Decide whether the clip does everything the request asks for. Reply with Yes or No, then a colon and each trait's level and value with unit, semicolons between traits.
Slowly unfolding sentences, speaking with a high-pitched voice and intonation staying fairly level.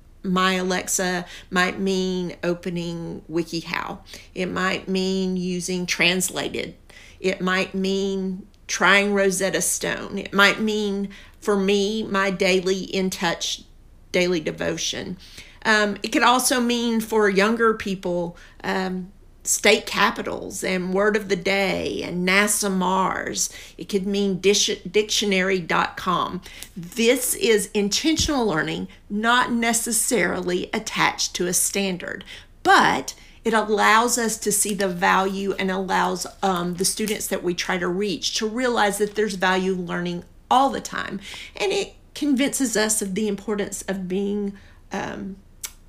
Yes: slow, 130 wpm; high, 195 Hz; narrow, 2.2 semitones